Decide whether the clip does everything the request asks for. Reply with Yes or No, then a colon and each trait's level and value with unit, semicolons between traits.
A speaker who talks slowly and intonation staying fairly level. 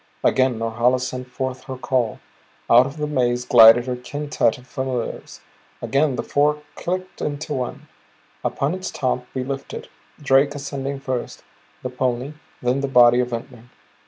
No: average, 155 wpm; narrow, 2.2 semitones